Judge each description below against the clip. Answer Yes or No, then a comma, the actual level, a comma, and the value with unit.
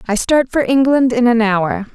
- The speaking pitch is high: Yes, high, 240 Hz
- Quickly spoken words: Yes, fast, 215 wpm